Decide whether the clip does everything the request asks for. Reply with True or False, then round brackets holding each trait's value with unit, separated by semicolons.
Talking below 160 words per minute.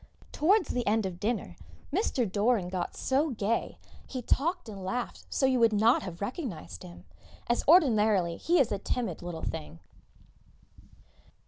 True (150 wpm)